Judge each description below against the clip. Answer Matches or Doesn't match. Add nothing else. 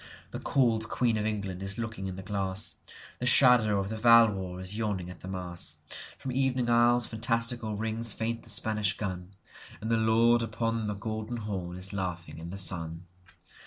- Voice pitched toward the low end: Matches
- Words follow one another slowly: Doesn't match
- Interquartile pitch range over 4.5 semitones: Doesn't match